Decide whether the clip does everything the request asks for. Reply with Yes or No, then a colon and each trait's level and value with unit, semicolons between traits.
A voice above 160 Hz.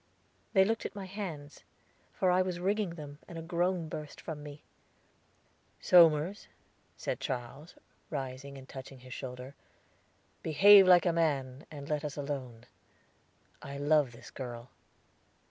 No: medium, 150 Hz